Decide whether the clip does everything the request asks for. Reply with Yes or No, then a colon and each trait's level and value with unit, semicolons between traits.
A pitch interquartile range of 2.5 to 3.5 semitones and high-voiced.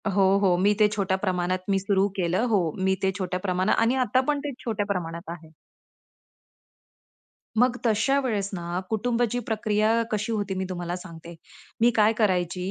Yes: average, 3.2 semitones; high, 195 Hz